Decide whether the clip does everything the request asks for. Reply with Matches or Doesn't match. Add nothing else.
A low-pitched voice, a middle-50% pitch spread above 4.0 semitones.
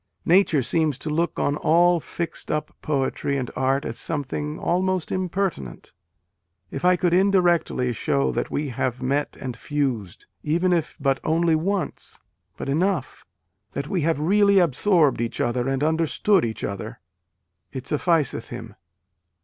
Doesn't match